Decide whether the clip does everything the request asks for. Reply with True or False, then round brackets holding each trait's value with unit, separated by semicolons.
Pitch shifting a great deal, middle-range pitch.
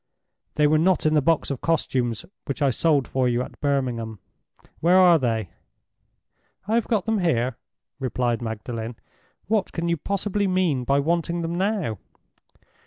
True (6.2 semitones; 150 Hz)